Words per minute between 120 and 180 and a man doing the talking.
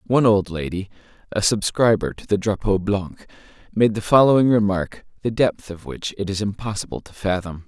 Yes: average, 170 wpm; male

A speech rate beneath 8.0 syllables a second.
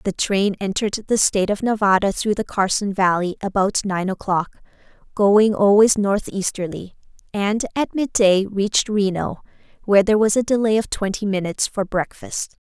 Yes: 5.0 syllables/s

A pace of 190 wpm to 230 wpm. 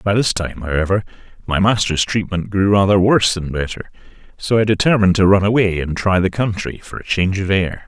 Yes: fast, 205 wpm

